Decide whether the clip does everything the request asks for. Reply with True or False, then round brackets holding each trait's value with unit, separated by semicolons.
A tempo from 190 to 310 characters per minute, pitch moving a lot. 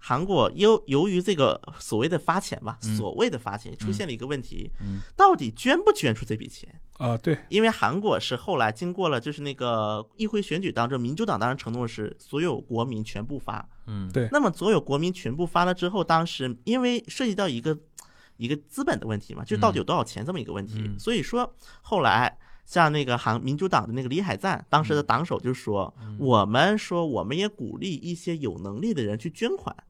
False (320 characters per minute; 8.5 semitones)